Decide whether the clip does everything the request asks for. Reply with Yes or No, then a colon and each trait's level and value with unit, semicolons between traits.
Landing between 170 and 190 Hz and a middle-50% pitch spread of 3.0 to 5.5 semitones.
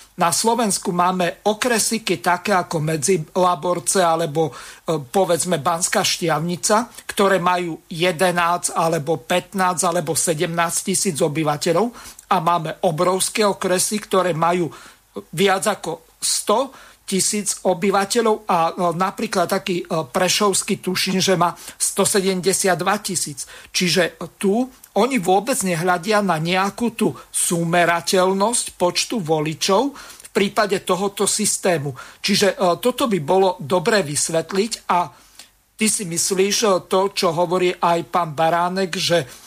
No: medium, 185 Hz; narrow, 2.6 semitones